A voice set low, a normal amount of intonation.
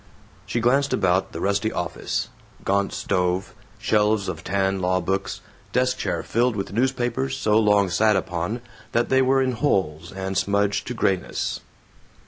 Yes: low, 100 Hz; average, 4.2 semitones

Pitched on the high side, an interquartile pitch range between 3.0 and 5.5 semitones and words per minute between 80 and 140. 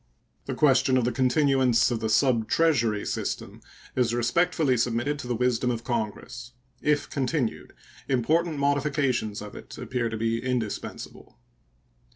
No: low, 125 Hz; average, 3.3 semitones; slow, 135 wpm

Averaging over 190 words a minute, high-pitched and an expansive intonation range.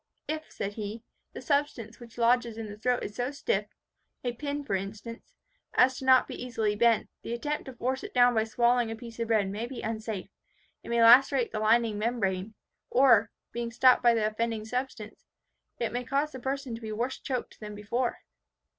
No: average, 200 wpm; high, 235 Hz; narrow, 2.5 semitones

